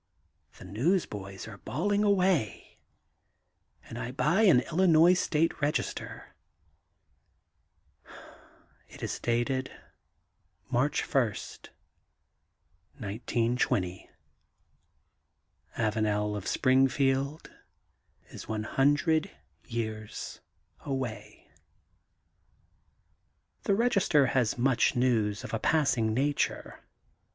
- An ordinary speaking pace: No, slow, 75 wpm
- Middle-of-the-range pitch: No, low, 130 Hz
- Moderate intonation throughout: No, wide, 6.0 semitones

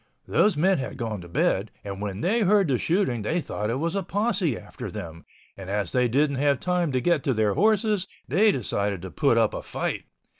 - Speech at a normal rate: No, fast, 220 wpm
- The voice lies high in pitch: No, medium, 140 Hz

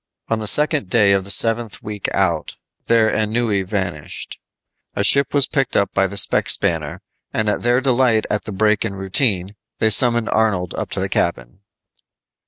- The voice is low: Yes, low, 105 Hz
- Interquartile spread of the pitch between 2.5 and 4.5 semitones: Yes, average, 3.2 semitones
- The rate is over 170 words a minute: Yes, average, 180 wpm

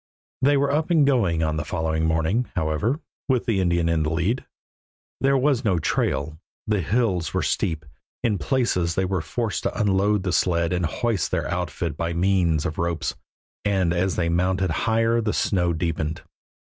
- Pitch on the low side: Yes, very low, 90 Hz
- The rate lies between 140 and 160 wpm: No, average, 175 wpm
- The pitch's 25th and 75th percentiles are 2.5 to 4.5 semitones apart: No, wide, 5.5 semitones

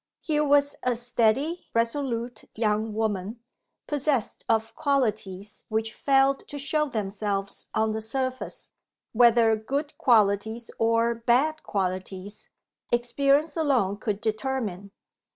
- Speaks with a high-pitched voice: Yes, high, 230 Hz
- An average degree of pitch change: Yes, average, 4.2 semitones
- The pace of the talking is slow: Yes, slow, 110 wpm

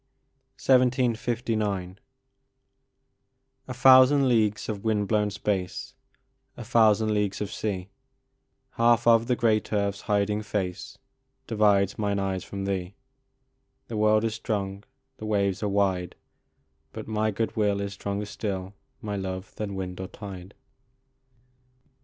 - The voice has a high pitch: No, low, 105 Hz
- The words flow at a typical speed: No, slow, 125 wpm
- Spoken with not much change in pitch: Yes, narrow, 2.1 semitones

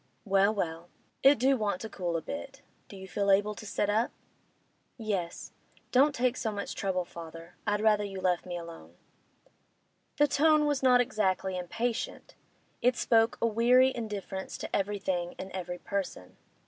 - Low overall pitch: No, high, 205 Hz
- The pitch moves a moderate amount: Yes, average, 4.4 semitones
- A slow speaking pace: No, average, 160 wpm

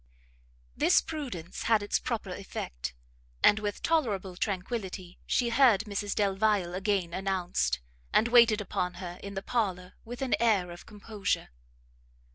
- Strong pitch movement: No, average, 3.5 semitones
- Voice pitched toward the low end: No, high, 200 Hz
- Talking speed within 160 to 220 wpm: No, slow, 135 wpm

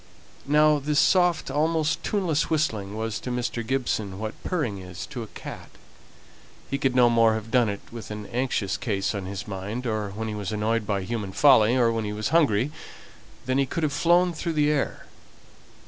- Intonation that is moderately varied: No, wide, 5.8 semitones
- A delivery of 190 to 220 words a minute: Yes, average, 195 wpm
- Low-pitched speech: Yes, low, 120 Hz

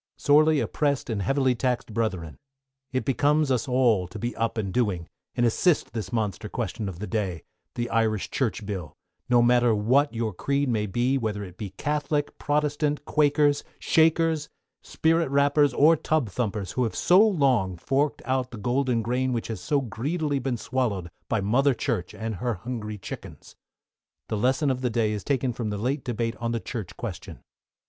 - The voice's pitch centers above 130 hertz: No, low, 120 Hz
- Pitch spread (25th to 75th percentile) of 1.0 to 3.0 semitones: No, average, 4.6 semitones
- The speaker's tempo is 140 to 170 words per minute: No, average, 180 wpm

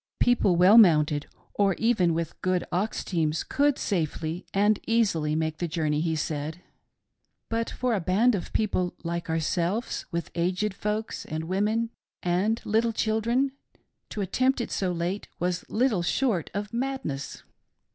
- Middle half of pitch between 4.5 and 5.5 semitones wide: Yes, average, 5.0 semitones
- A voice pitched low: No, medium, 185 Hz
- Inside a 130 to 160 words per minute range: Yes, average, 150 wpm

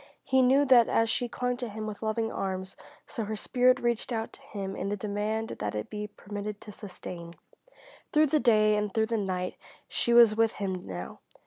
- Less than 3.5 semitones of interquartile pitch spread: Yes, average, 2.8 semitones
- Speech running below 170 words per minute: No, fast, 205 wpm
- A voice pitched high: Yes, high, 215 Hz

